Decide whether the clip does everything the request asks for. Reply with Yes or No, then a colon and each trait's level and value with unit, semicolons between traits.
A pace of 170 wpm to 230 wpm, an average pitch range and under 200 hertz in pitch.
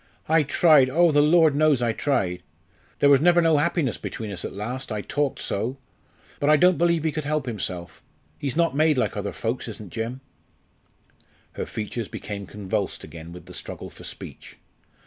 No: average, 185 wpm; wide, 6.5 semitones; low, 135 Hz